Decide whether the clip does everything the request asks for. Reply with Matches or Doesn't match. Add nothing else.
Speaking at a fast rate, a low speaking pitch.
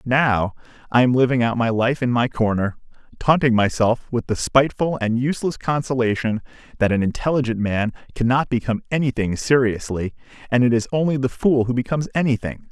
Doesn't match